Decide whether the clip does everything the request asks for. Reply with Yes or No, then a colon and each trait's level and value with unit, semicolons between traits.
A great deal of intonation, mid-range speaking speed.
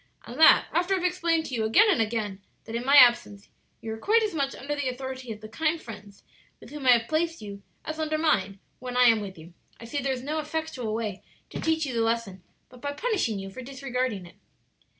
No: wide, 6.0 semitones; fast, 240 wpm